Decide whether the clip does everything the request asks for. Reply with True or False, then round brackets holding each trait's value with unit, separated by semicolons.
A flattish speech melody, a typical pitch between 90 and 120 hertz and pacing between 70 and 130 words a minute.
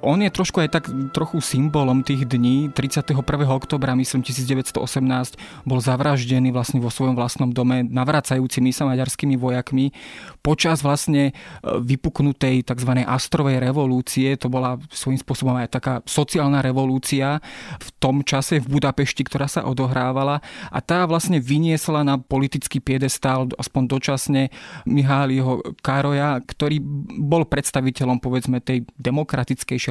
False (2.0 semitones; 135 Hz; 125 wpm)